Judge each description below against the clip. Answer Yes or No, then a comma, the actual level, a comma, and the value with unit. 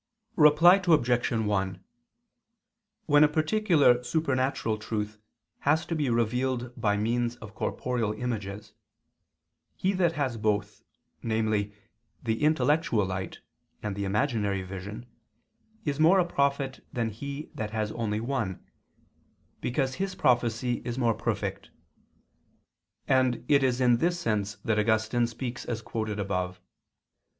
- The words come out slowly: Yes, slow, 125 wpm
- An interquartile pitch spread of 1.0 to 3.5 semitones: No, average, 4.6 semitones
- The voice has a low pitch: Yes, low, 120 Hz